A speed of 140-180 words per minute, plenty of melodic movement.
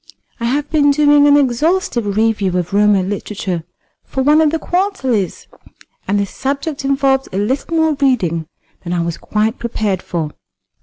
Yes: average, 160 wpm; wide, 6.5 semitones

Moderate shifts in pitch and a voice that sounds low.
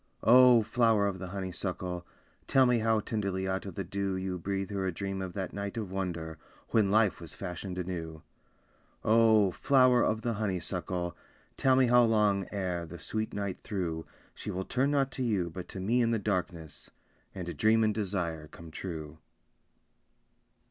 Yes: average, 3.6 semitones; very low, 95 Hz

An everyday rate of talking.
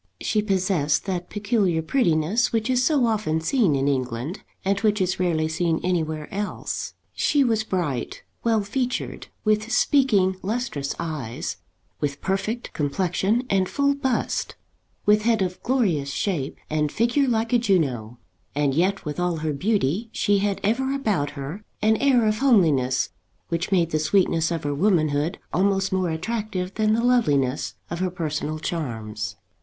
Yes: average, 155 wpm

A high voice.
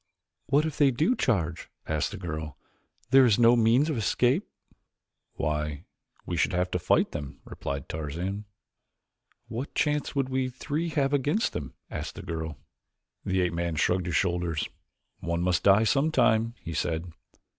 No: very low, 95 Hz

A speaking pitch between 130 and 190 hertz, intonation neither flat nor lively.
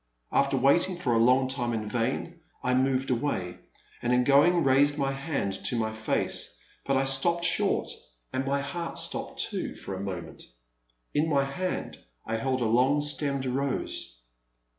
Yes: low, 135 Hz; average, 3.0 semitones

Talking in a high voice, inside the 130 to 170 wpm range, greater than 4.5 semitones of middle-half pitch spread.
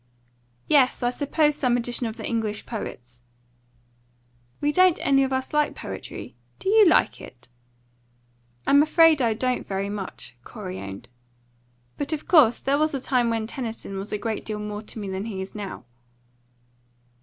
Yes: high, 235 Hz; average, 165 wpm; wide, 5.5 semitones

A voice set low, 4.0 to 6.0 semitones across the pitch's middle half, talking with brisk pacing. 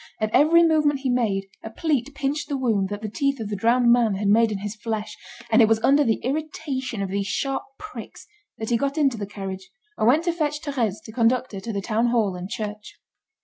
No: high, 230 Hz; average, 4.9 semitones; fast, 230 wpm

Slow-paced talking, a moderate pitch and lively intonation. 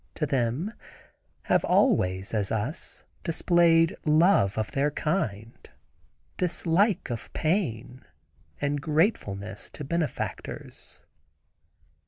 Yes: slow, 90 wpm; medium, 150 Hz; wide, 7.1 semitones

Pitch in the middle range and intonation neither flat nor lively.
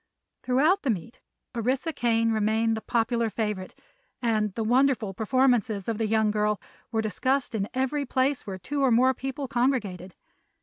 No: high, 230 Hz; average, 3.4 semitones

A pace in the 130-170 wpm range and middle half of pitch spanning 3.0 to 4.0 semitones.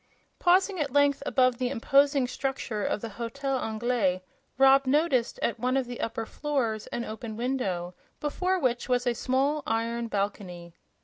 Yes: average, 160 wpm; average, 3.5 semitones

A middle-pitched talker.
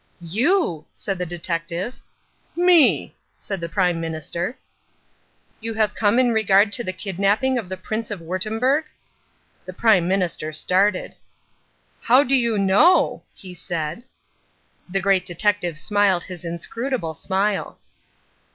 No: high, 195 Hz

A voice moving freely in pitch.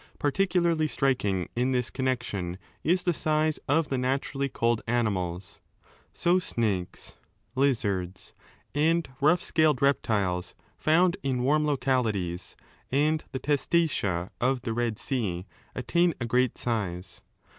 Yes: wide, 6.5 semitones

